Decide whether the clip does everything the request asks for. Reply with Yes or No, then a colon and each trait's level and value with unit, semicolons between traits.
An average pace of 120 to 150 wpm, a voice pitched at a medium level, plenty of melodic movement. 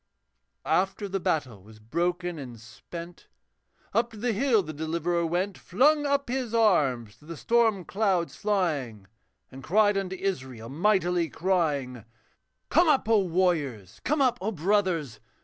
Yes: average, 145 wpm; medium, 180 Hz; wide, 6.3 semitones